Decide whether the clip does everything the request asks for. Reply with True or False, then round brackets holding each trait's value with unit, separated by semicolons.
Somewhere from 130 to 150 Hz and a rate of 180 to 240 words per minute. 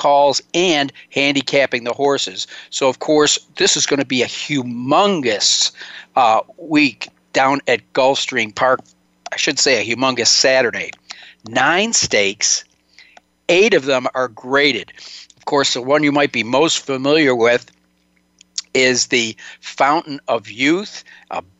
False (135 Hz; 140 wpm)